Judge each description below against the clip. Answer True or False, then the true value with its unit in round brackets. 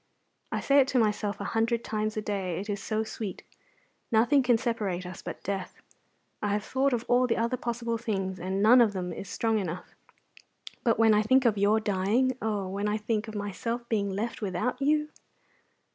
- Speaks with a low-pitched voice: False (215 Hz)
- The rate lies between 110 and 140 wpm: False (200 wpm)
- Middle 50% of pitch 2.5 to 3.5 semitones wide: True (2.8 semitones)